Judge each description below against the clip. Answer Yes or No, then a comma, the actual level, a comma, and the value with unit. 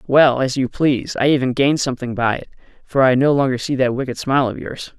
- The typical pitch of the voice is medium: No, low, 130 Hz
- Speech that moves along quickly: Yes, fast, 240 wpm